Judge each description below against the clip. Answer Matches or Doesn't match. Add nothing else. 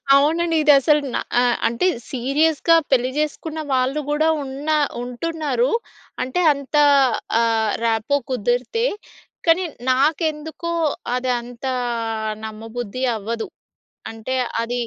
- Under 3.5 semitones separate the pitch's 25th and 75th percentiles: Doesn't match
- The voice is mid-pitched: Doesn't match